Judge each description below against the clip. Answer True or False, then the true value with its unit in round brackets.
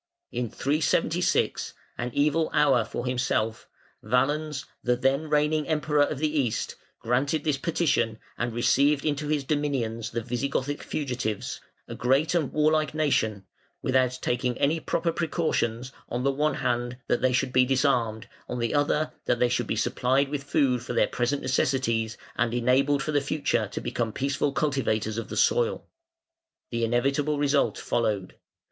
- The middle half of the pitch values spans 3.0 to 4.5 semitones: True (3.5 semitones)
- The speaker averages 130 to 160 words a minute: True (155 wpm)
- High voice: False (135 Hz)